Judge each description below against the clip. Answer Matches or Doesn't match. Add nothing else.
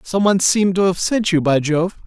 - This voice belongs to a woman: Doesn't match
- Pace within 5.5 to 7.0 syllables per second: Matches